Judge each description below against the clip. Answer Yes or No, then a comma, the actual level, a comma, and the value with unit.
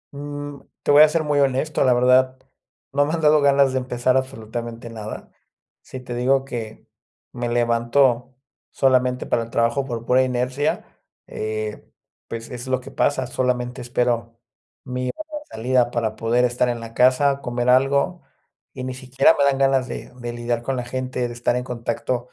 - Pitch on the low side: Yes, low, 125 Hz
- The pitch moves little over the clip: Yes, narrow, 2.1 semitones